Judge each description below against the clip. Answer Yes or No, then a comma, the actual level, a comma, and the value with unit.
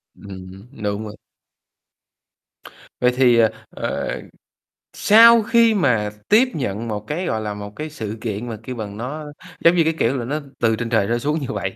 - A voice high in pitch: No, low, 120 Hz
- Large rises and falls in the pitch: Yes, wide, 6.5 semitones